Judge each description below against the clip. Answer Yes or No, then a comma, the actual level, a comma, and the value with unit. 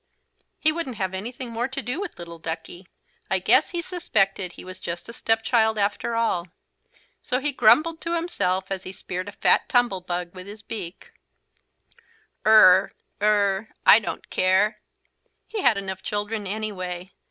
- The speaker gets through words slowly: No, average, 165 wpm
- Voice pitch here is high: Yes, high, 205 Hz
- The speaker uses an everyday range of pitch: Yes, average, 4.2 semitones